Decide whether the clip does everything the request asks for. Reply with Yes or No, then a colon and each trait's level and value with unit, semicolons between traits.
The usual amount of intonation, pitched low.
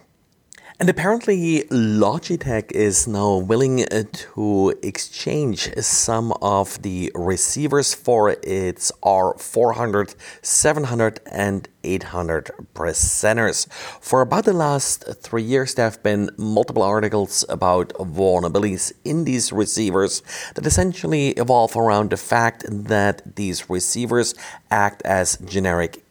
Yes: average, 4.2 semitones; low, 105 Hz